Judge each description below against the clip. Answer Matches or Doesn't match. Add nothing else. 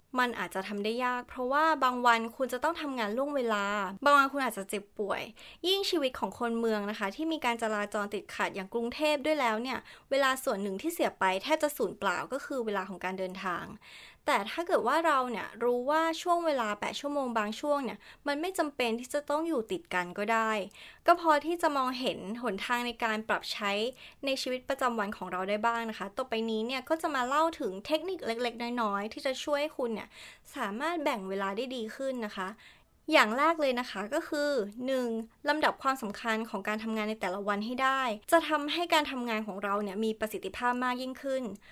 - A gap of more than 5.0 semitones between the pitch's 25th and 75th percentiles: Matches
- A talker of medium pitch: Doesn't match